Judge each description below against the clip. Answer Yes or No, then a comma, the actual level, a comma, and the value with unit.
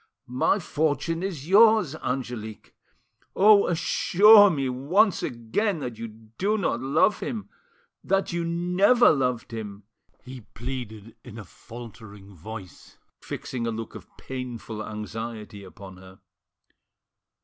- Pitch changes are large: Yes, wide, 8.4 semitones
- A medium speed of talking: No, slow, 115 wpm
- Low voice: Yes, low, 125 Hz